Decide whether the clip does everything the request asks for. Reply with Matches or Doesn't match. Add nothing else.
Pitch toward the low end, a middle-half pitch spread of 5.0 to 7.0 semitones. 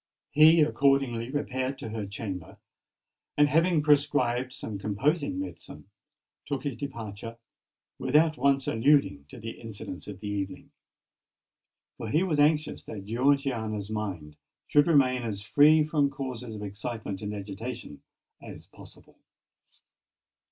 Matches